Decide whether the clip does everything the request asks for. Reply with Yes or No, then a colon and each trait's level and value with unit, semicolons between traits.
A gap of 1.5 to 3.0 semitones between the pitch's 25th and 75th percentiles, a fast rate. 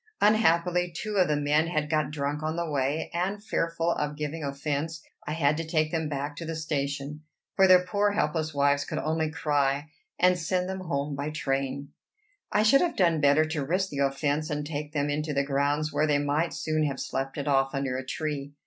Yes: narrow, 2.6 semitones; fast, 210 wpm